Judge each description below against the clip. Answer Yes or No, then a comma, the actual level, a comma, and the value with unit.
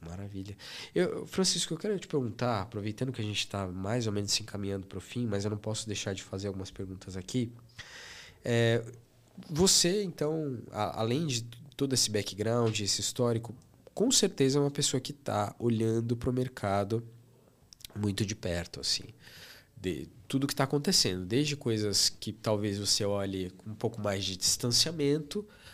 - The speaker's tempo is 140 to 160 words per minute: No, average, 170 wpm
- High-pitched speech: No, low, 115 Hz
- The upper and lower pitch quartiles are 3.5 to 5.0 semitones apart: Yes, average, 4.5 semitones